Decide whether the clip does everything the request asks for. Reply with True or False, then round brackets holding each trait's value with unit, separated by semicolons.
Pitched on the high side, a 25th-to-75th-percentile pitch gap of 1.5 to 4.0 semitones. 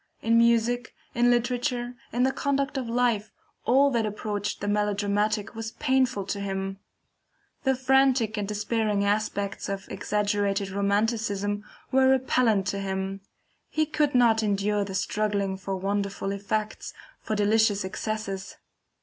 True (210 Hz; 3.2 semitones)